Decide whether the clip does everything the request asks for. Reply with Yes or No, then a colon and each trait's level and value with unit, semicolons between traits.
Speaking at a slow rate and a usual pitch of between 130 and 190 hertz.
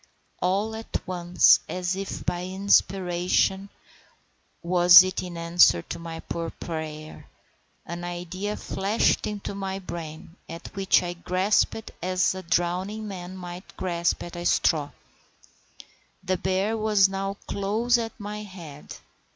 Yes: slow, 125 wpm; medium, 185 Hz